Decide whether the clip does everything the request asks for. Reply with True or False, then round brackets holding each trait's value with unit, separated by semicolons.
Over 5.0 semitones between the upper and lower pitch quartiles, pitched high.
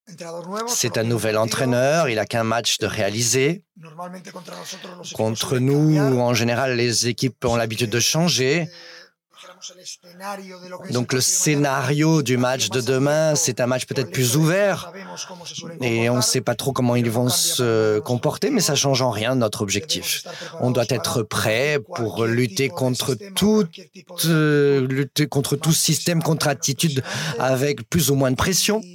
False (5.5 semitones; 135 Hz)